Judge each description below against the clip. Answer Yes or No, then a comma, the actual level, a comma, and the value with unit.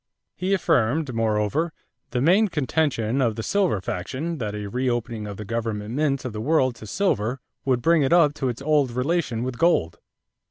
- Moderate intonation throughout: No, wide, 5.7 semitones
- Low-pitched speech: Yes, low, 125 Hz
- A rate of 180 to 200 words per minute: Yes, average, 185 wpm